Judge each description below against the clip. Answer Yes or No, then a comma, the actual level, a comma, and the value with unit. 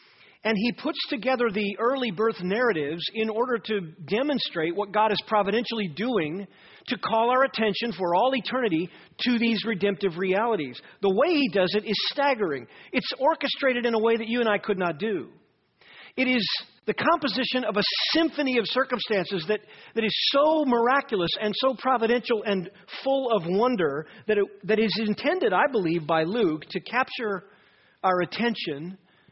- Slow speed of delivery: No, average, 165 wpm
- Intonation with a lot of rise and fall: No, average, 4.1 semitones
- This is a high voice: Yes, high, 220 Hz